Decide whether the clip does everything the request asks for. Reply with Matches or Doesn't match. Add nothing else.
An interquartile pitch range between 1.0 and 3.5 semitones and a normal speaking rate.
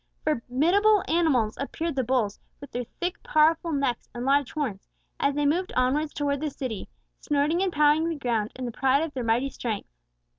Doesn't match